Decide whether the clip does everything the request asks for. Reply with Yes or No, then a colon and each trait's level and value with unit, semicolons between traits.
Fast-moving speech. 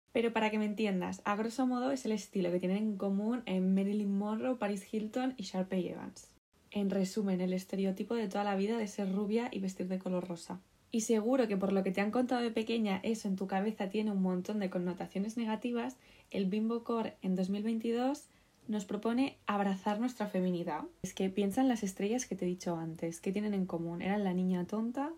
Yes: fast, 210 wpm